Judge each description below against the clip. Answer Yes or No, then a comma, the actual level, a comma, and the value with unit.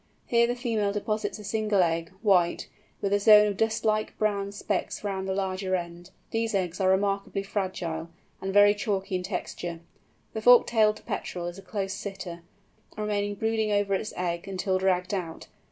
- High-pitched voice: Yes, high, 200 Hz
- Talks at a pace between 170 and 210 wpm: Yes, average, 175 wpm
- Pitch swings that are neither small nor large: No, narrow, 2.2 semitones